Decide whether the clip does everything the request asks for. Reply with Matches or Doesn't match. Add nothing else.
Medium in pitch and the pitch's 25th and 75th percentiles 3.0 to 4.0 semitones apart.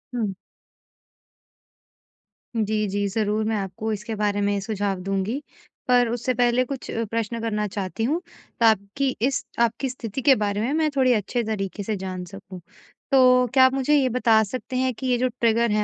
Doesn't match